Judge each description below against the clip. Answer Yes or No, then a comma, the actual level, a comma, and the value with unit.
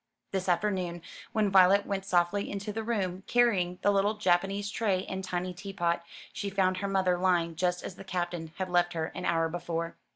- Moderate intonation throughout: No, narrow, 2.3 semitones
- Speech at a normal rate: Yes, average, 190 wpm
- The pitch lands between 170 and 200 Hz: Yes, medium, 185 Hz